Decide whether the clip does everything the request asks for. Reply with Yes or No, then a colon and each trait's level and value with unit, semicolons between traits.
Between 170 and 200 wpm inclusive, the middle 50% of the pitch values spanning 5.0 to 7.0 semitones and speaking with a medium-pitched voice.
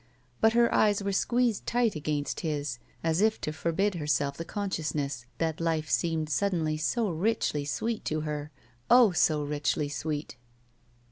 No: average, 155 wpm; average, 5.3 semitones; medium, 160 Hz